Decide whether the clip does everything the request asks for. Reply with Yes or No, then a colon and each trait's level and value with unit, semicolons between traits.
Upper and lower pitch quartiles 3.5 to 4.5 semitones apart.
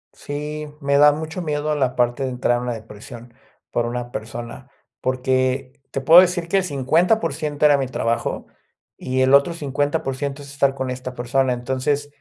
No: average, 2.8 semitones